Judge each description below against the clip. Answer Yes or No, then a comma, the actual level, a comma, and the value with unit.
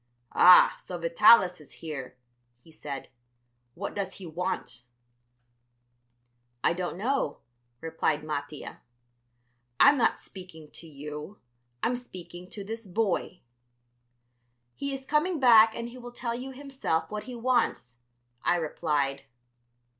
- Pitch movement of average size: No, wide, 7.3 semitones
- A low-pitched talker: No, medium, 185 Hz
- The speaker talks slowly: Yes, slow, 125 wpm